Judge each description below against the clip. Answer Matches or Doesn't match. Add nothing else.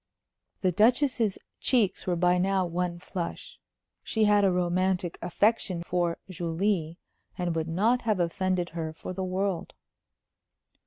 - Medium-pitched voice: Matches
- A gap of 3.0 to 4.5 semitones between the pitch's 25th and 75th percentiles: Doesn't match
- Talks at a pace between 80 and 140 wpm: Matches